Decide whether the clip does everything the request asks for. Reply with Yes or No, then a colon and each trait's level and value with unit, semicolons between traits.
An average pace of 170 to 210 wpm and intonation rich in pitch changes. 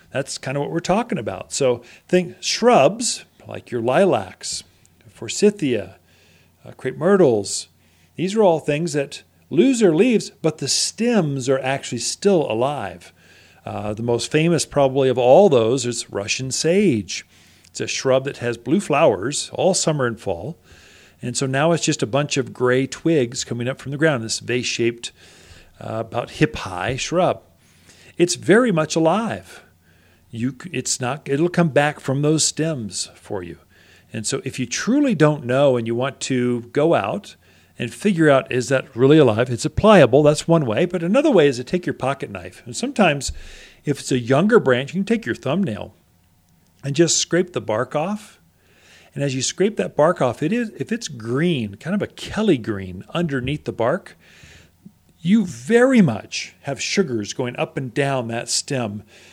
Yes: average, 180 wpm; wide, 6.6 semitones